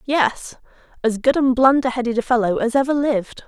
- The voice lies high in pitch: Yes, very high, 255 Hz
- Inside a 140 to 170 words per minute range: No, average, 190 wpm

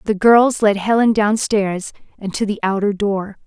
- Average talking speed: Yes, average, 175 wpm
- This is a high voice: Yes, high, 205 Hz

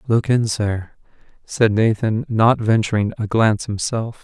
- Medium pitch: No, low, 110 Hz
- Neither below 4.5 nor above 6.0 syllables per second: No, 4.3 syllables/s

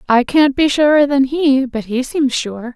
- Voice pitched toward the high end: Yes, very high, 270 Hz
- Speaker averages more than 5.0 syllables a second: No, 4.3 syllables/s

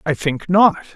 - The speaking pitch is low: No, medium, 170 Hz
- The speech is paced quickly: No, average, 190 wpm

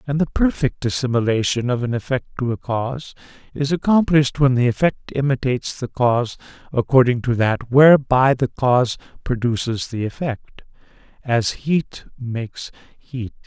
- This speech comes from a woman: No, male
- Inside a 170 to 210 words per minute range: No, average, 140 wpm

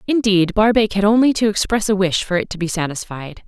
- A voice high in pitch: Yes, high, 200 Hz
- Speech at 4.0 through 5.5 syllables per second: No, 5.7 syllables/s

